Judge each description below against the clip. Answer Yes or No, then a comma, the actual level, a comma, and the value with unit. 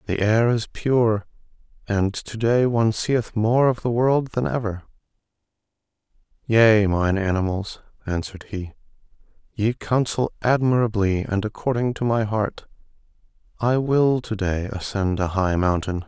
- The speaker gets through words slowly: Yes, slow, 130 wpm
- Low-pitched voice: Yes, low, 110 Hz